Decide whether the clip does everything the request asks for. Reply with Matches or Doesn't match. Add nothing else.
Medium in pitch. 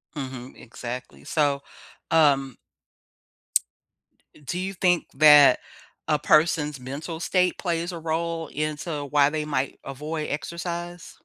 Matches